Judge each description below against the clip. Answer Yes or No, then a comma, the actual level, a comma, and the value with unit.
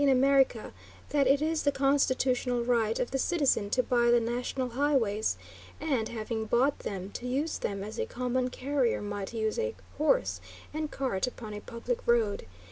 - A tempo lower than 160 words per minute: No, average, 175 wpm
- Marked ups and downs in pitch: No, average, 3.7 semitones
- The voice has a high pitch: Yes, very high, 250 Hz